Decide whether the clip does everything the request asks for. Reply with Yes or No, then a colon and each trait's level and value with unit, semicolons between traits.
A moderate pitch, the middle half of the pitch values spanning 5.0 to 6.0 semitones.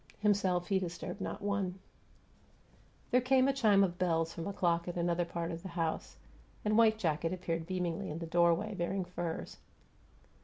No: medium, 180 Hz; average, 3.0 semitones